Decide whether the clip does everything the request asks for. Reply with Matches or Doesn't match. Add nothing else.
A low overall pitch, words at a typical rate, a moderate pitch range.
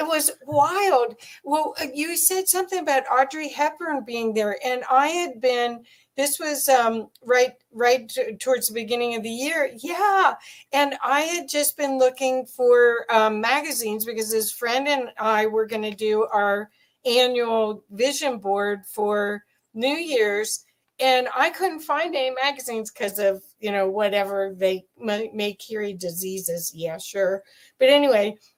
Doesn't match